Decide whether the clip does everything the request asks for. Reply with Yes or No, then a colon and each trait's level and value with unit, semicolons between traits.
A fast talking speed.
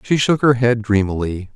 No: average, 195 wpm